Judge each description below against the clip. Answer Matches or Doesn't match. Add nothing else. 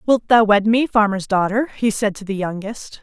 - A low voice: Doesn't match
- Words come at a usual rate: Doesn't match